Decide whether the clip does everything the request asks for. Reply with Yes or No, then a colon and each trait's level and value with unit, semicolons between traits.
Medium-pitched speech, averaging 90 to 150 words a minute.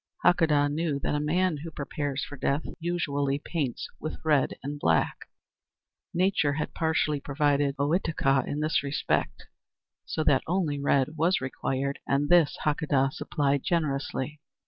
Yes: medium, 145 Hz; average, 140 wpm